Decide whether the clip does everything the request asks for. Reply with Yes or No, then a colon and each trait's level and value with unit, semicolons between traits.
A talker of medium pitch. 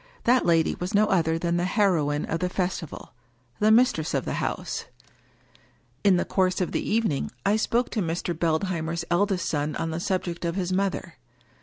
Yes: medium, 180 Hz